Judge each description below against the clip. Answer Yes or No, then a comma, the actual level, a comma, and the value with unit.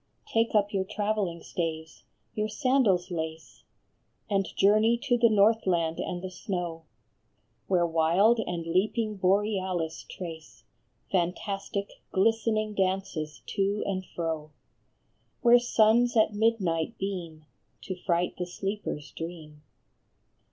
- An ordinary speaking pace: No, slow, 115 wpm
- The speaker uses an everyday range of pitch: Yes, average, 4.0 semitones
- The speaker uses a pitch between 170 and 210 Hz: Yes, high, 190 Hz